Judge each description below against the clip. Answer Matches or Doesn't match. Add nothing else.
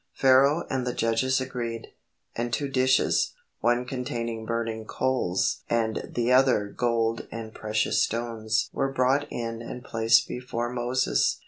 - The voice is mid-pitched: Doesn't match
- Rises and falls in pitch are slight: Matches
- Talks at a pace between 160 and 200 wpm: Doesn't match